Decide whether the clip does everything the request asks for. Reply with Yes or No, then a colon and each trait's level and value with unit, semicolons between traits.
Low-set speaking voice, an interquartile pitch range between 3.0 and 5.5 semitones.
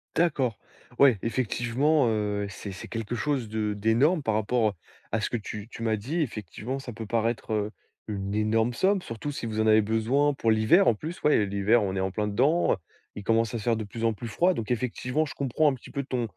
Yes: low, 115 Hz; average, 3.7 semitones